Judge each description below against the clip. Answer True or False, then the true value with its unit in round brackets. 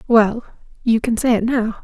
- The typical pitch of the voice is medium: False (230 Hz)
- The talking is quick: False (165 wpm)